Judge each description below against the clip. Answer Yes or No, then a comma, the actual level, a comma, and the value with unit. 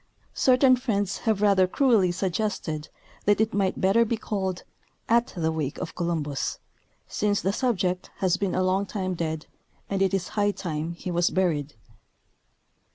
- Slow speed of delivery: No, average, 160 wpm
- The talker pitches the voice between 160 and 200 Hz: Yes, high, 190 Hz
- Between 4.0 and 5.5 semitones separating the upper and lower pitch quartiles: No, average, 3.2 semitones